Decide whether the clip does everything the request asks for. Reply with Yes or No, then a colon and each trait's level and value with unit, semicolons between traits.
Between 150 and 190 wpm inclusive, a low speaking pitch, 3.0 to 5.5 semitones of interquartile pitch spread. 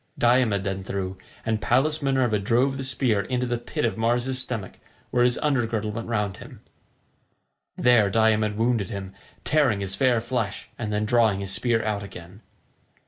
Yes: average, 170 wpm; low, 115 Hz; average, 3.4 semitones